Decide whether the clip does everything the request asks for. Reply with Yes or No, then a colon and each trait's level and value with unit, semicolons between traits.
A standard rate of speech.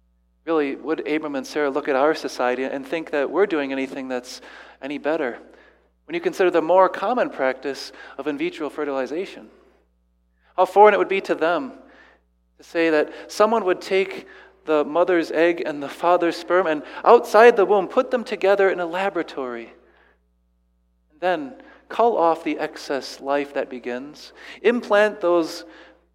Yes: average, 160 wpm